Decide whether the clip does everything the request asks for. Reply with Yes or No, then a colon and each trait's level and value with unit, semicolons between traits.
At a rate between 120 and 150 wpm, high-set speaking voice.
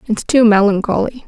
Yes: average, 140 wpm; high, 220 Hz